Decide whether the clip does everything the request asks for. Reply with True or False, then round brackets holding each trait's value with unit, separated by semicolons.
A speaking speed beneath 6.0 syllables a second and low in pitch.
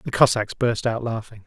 True (5.2 syllables/s; 115 Hz)